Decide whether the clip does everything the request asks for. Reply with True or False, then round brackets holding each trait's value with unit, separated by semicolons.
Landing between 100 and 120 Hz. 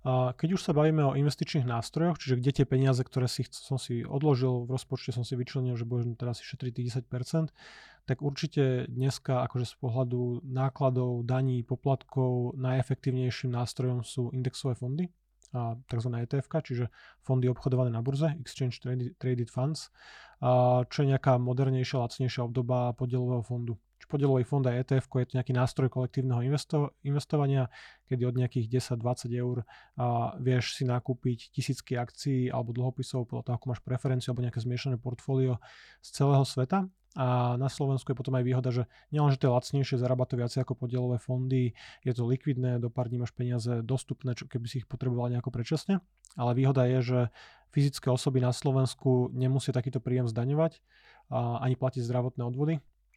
False (130 Hz)